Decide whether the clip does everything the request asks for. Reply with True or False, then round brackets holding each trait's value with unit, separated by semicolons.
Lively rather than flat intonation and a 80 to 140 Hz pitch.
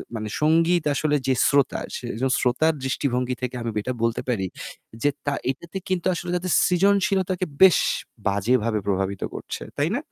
True (7.0 semitones; 135 Hz)